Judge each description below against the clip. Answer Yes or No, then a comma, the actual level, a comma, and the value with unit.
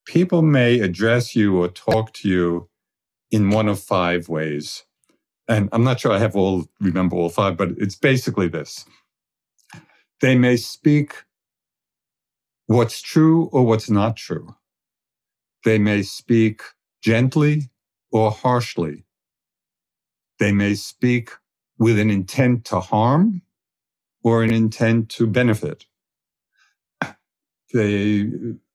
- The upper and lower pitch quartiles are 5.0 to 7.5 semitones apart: No, average, 3.6 semitones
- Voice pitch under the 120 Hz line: Yes, low, 110 Hz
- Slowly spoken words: Yes, slow, 115 wpm